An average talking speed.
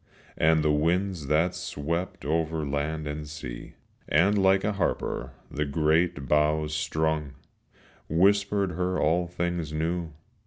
No: slow, 125 wpm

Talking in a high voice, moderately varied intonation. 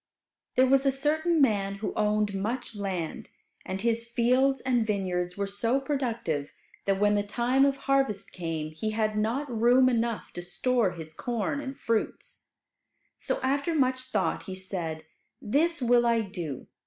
Yes: high, 230 Hz; average, 5.0 semitones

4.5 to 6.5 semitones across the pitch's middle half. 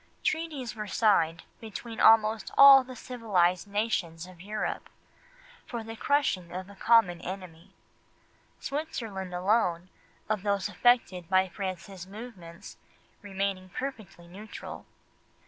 No: average, 3.7 semitones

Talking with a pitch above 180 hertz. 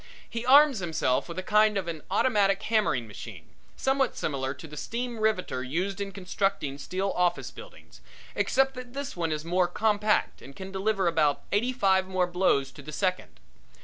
Yes: high, 190 Hz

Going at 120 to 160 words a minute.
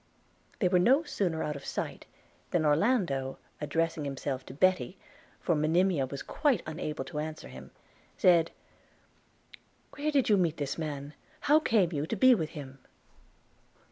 Yes: average, 155 wpm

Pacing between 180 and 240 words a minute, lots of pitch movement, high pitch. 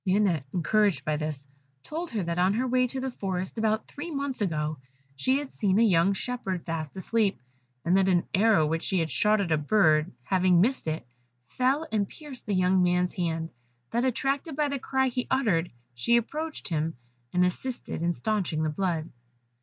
Yes: average, 190 wpm; wide, 6.9 semitones; high, 195 Hz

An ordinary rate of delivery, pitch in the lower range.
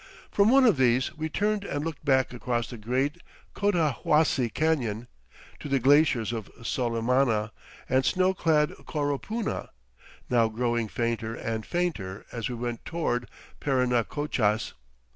No: slow, 130 wpm; low, 130 Hz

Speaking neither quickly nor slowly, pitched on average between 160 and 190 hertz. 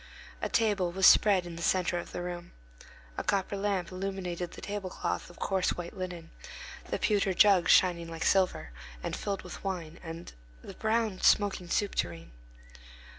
Yes: average, 165 wpm; medium, 185 Hz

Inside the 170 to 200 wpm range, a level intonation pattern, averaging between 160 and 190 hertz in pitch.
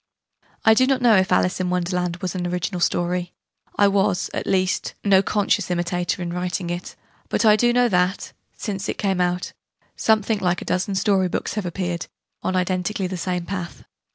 Yes: average, 185 wpm; narrow, 2.1 semitones; medium, 185 Hz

